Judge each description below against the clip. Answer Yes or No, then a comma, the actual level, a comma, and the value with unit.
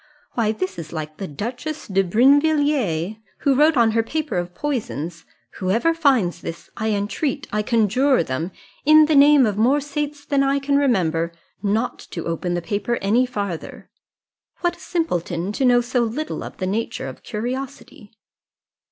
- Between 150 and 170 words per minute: Yes, average, 165 wpm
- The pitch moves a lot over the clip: Yes, wide, 7.1 semitones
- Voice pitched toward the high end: Yes, high, 230 Hz